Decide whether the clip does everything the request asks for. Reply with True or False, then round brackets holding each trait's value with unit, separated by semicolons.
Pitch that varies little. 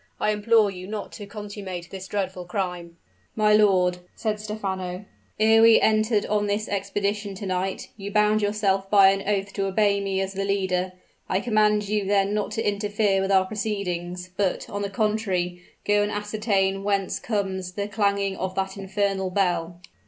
True (1.7 semitones)